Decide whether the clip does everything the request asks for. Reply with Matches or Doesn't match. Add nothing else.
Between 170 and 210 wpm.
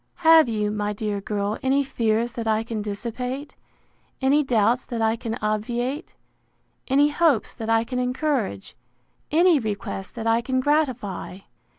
Doesn't match